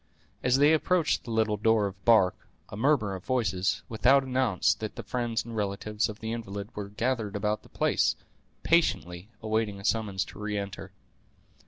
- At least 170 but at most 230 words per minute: Yes, average, 175 wpm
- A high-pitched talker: No, low, 110 Hz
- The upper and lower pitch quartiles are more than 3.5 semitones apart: No, average, 2.9 semitones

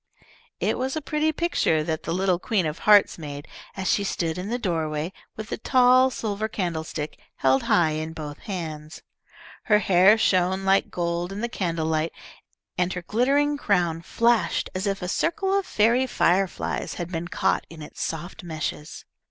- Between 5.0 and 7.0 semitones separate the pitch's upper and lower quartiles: Yes, average, 5.3 semitones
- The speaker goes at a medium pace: Yes, average, 170 wpm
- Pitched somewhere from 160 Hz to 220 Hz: Yes, medium, 185 Hz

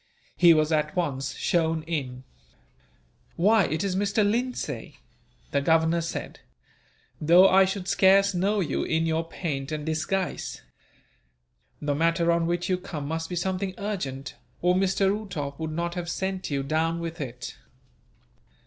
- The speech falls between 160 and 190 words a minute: No, average, 150 wpm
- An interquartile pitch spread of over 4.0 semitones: No, average, 3.4 semitones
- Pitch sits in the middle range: Yes, medium, 170 Hz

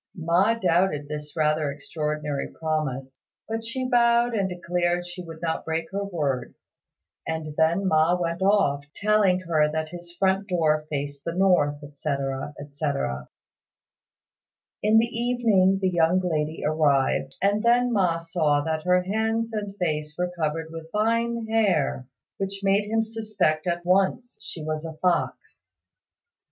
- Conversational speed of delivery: Yes, average, 145 wpm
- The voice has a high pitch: No, medium, 170 Hz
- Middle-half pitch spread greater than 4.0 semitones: Yes, average, 4.6 semitones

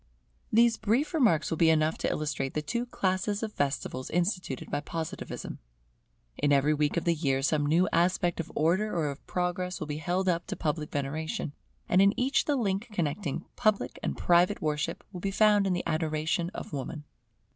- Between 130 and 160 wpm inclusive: No, average, 190 wpm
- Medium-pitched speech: Yes, medium, 170 Hz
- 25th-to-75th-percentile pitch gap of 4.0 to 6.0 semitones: Yes, average, 4.4 semitones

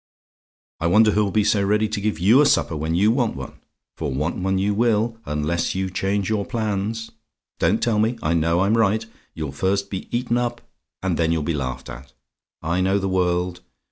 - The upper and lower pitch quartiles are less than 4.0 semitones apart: No, average, 4.4 semitones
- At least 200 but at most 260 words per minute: Yes, fast, 205 wpm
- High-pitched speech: No, very low, 95 Hz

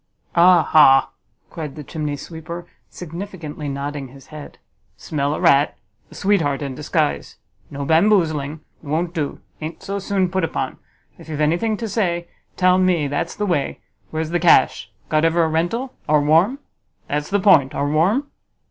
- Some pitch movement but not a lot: Yes, average, 3.7 semitones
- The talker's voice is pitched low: No, medium, 160 Hz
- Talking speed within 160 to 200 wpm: Yes, average, 170 wpm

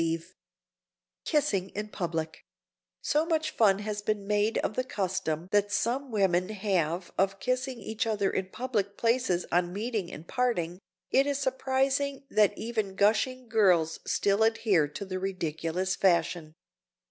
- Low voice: No, high, 205 Hz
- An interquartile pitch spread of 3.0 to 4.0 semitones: No, average, 4.5 semitones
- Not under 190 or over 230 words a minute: No, average, 145 wpm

